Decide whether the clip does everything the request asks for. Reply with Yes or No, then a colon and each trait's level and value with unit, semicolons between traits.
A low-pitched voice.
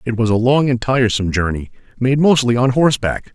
Yes: low, 120 Hz